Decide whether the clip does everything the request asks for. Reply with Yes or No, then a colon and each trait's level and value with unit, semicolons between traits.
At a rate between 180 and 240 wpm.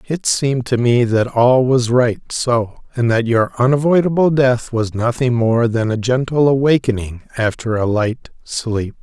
No: average, 165 wpm